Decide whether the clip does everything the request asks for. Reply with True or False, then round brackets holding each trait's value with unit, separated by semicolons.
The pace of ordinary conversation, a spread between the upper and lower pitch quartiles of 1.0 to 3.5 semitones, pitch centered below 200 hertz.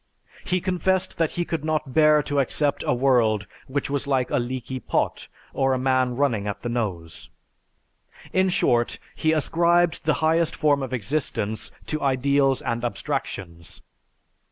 False (155 wpm; 4.3 semitones; 135 Hz)